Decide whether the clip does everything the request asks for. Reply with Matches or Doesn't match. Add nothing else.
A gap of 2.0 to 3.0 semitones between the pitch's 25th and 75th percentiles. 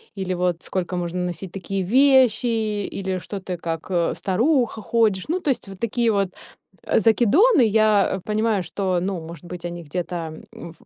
Doesn't match